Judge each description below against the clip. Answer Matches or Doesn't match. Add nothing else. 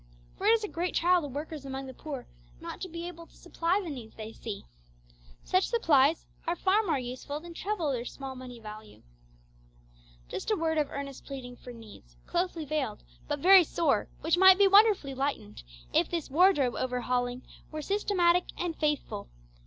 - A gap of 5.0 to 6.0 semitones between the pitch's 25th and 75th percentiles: Matches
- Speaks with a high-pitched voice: Matches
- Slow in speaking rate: Doesn't match